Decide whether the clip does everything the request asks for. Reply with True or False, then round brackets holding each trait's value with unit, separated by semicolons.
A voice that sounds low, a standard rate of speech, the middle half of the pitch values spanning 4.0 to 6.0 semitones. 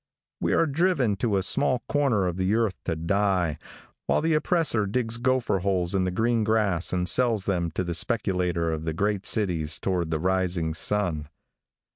True (95 Hz; 180 wpm; 4.6 semitones)